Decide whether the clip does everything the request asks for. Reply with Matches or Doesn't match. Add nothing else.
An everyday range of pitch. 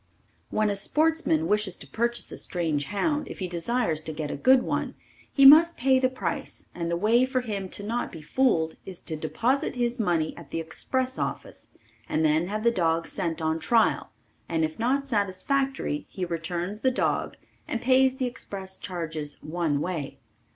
Doesn't match